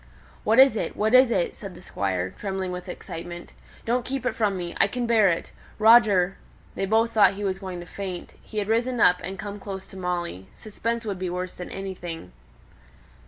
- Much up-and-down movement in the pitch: No, average, 3.7 semitones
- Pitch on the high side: Yes, high, 195 Hz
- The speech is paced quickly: Yes, fast, 210 wpm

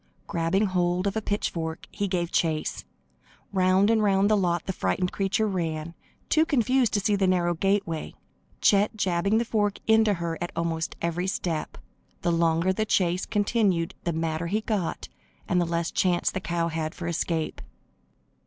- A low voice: No, medium, 180 Hz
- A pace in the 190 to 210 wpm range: No, average, 170 wpm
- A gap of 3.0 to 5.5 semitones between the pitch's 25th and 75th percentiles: Yes, average, 3.4 semitones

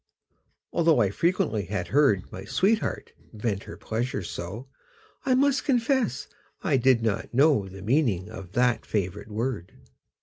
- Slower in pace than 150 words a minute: Yes, average, 140 wpm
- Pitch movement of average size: No, wide, 7.2 semitones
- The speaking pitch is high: No, low, 115 Hz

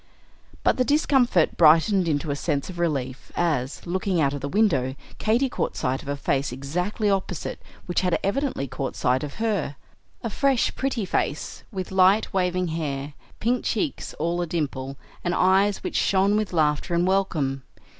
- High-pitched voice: No, medium, 175 Hz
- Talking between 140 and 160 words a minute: No, average, 170 wpm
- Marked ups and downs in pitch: Yes, wide, 5.9 semitones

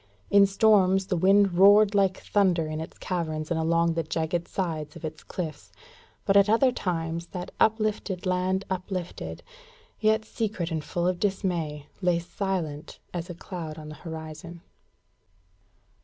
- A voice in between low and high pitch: Yes, medium, 180 Hz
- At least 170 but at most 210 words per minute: No, average, 150 wpm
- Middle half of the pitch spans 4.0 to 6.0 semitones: No, average, 3.2 semitones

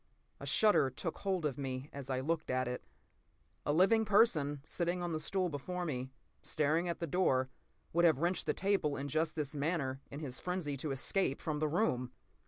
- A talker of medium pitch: Yes, medium, 155 Hz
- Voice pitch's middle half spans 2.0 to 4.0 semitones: No, average, 4.6 semitones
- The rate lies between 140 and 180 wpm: No, average, 195 wpm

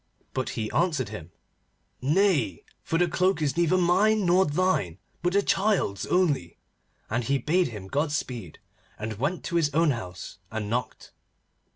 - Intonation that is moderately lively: No, wide, 8.4 semitones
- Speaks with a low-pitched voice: No, medium, 150 Hz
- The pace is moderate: Yes, average, 155 wpm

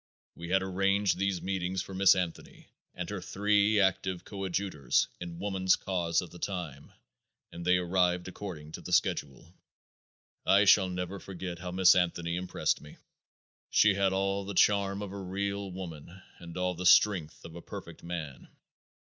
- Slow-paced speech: No, average, 165 wpm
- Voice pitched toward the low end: Yes, very low, 95 Hz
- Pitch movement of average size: No, narrow, 2.1 semitones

